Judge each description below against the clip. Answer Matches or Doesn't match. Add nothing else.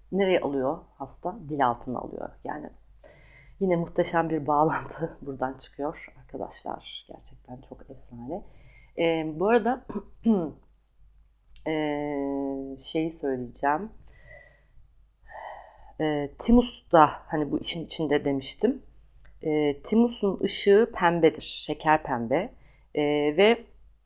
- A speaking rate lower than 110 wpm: Matches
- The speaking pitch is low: Doesn't match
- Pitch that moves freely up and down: Doesn't match